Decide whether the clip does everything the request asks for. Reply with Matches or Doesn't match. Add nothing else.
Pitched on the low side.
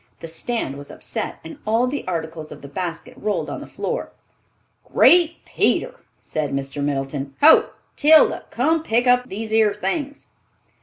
Doesn't match